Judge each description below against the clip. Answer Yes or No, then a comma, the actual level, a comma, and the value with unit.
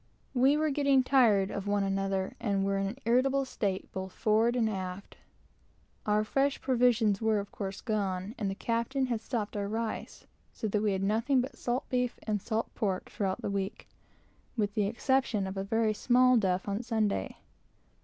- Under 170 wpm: No, average, 185 wpm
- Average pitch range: Yes, average, 3.8 semitones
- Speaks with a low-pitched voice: No, high, 215 Hz